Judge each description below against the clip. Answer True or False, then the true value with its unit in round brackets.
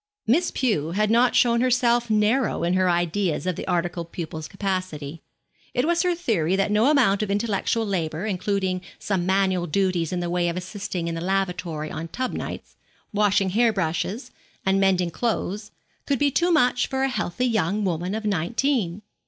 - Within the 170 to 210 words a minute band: True (175 wpm)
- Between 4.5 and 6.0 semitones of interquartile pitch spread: True (4.8 semitones)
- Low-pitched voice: False (195 Hz)